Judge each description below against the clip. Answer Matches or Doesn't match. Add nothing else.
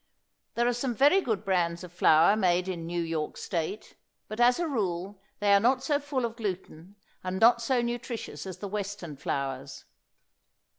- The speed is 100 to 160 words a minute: Doesn't match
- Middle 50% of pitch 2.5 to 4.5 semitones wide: Doesn't match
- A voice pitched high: Matches